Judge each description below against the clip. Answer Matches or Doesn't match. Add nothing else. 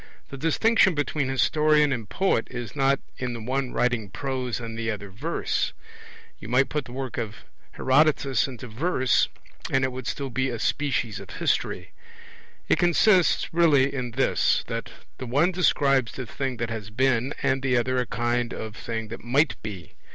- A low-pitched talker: Matches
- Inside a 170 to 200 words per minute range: Matches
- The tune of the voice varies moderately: Matches